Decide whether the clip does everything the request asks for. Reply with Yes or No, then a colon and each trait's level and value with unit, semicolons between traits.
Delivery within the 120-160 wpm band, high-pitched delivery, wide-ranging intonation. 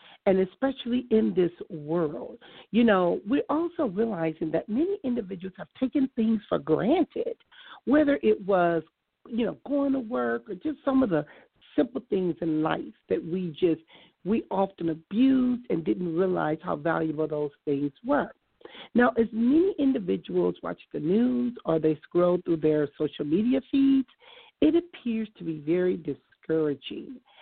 Yes: average, 155 wpm; high, 200 Hz; wide, 8.4 semitones